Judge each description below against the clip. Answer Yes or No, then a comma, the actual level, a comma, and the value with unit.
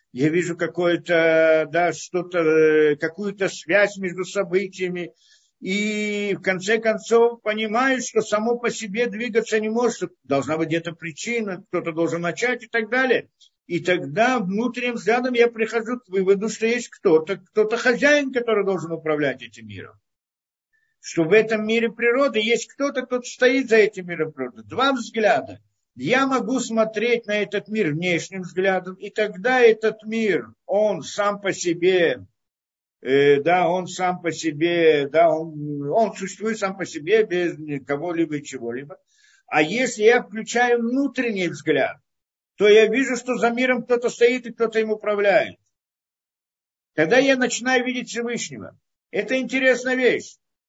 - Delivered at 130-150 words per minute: Yes, average, 145 wpm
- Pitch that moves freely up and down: Yes, wide, 5.9 semitones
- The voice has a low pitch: No, high, 205 Hz